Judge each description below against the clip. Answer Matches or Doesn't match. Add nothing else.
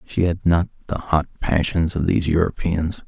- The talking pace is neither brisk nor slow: Matches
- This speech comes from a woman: Doesn't match